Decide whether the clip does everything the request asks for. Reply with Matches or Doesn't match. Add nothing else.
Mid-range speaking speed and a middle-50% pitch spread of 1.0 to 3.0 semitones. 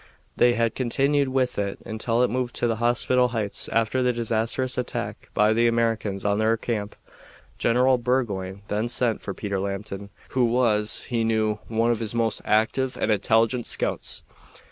Matches